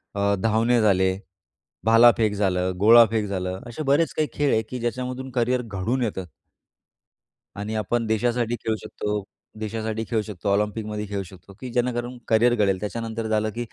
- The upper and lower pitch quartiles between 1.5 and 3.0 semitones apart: Yes, average, 2.7 semitones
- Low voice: Yes, low, 110 Hz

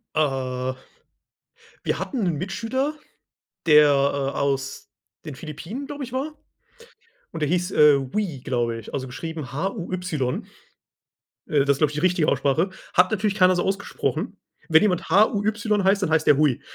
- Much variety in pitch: Yes, wide, 6.0 semitones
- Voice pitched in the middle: Yes, medium, 160 Hz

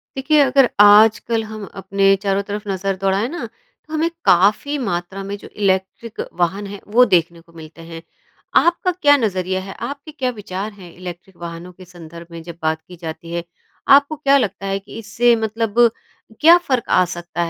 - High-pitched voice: Yes, high, 195 Hz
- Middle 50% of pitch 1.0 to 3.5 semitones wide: No, wide, 5.5 semitones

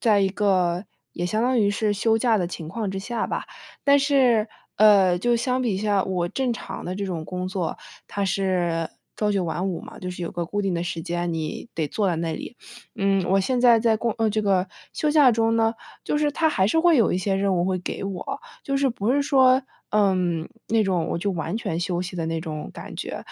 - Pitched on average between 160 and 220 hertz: Yes, high, 195 Hz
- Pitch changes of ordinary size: Yes, average, 4.3 semitones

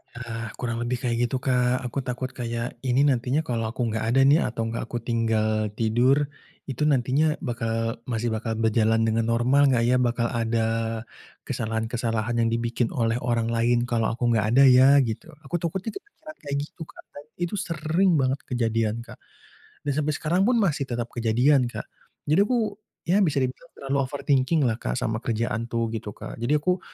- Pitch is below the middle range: Yes, low, 120 Hz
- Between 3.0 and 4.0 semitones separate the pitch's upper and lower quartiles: Yes, average, 3.4 semitones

